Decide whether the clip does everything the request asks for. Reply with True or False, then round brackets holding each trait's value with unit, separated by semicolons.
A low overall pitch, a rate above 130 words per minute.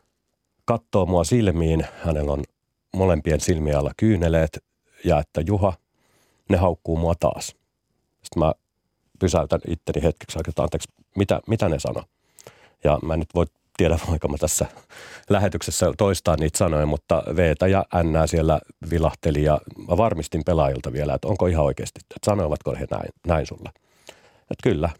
True (80 Hz; 150 wpm)